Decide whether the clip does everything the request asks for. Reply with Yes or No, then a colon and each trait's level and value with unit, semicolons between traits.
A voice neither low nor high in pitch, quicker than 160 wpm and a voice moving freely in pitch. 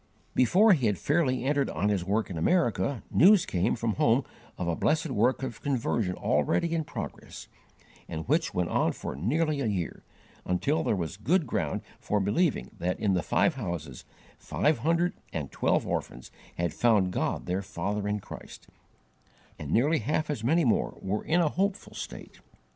No: low, 115 Hz; average, 175 wpm; wide, 8.6 semitones